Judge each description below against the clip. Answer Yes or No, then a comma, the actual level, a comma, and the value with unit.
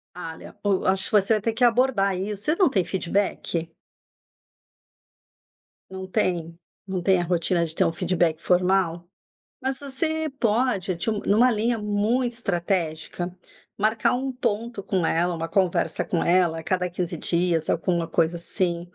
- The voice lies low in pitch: No, high, 190 Hz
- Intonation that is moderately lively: Yes, average, 4.2 semitones